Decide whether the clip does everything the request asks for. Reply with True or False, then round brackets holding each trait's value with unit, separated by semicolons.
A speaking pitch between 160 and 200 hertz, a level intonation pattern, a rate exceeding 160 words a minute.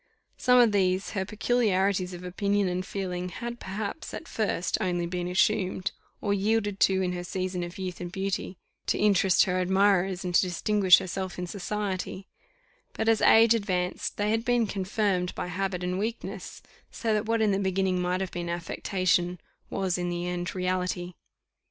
True (190 Hz; 2.3 semitones; 175 wpm)